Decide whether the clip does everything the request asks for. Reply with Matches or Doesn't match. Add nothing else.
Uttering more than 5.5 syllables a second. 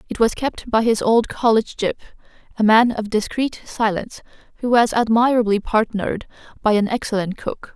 Doesn't match